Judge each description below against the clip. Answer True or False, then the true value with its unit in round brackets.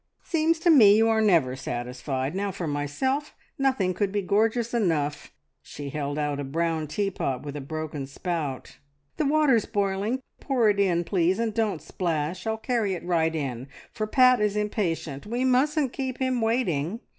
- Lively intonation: True (7.3 semitones)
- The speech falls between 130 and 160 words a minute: False (170 wpm)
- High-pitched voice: True (195 Hz)